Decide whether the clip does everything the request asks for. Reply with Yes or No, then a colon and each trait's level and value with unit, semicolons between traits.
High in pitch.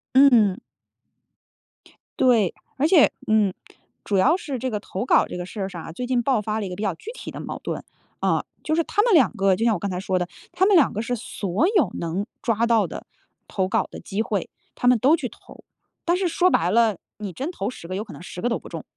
Yes: high, 220 Hz